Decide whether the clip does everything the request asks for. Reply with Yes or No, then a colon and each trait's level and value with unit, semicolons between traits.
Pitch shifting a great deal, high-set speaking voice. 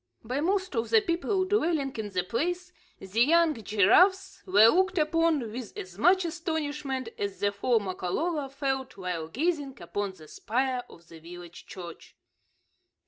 Yes: wide, 8.8 semitones; very high, 265 Hz